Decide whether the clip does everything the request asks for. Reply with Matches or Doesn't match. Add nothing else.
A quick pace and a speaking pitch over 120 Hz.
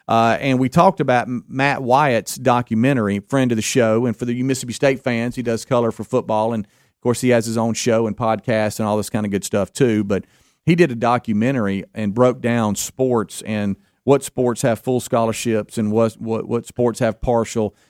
Doesn't match